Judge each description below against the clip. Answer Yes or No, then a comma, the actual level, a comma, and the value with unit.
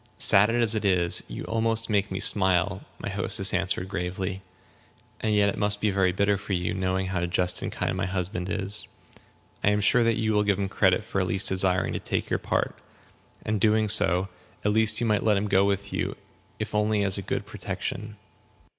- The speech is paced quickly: Yes, fast, 210 wpm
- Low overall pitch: Yes, low, 100 Hz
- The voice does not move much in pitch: Yes, narrow, 2.1 semitones